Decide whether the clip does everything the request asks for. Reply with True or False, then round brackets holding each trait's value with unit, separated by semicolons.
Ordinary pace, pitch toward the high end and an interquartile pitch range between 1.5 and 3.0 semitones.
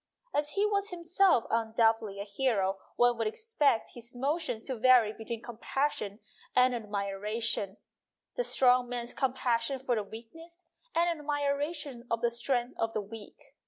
False (150 wpm; 240 Hz; 4.4 semitones)